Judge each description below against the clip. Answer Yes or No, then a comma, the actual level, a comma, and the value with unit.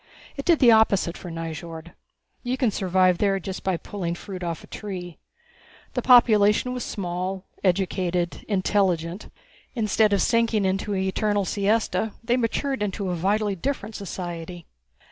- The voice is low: No, high, 195 Hz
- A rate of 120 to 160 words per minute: Yes, average, 145 wpm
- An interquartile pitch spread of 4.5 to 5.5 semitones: No, average, 3.4 semitones